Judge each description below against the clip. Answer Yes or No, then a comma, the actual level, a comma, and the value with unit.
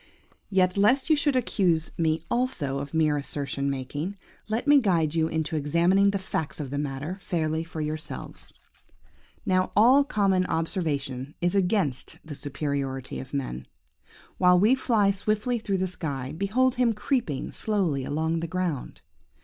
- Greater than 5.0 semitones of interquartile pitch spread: Yes, wide, 5.6 semitones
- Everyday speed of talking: Yes, average, 150 wpm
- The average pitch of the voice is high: No, medium, 170 Hz